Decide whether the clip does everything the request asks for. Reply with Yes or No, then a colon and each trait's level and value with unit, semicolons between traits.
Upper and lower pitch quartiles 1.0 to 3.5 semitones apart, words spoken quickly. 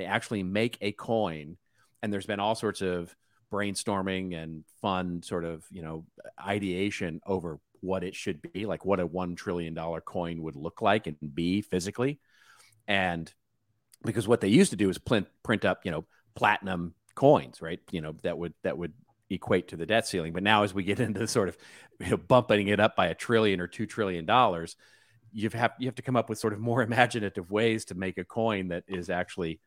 No: average, 4.1 semitones; fast, 210 wpm